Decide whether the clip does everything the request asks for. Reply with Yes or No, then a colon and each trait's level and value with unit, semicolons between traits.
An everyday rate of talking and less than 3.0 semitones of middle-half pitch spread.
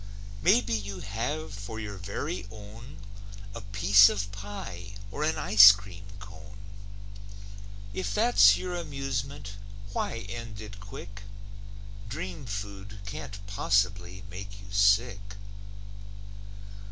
No: slow, 110 wpm; narrow, 2.6 semitones